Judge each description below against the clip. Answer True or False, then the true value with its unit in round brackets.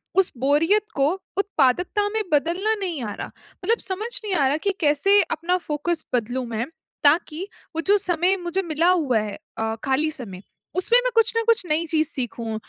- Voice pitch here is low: False (320 Hz)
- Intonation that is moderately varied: False (6.2 semitones)